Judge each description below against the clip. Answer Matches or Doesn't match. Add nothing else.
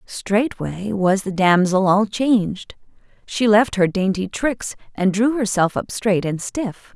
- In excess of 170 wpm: Doesn't match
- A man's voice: Doesn't match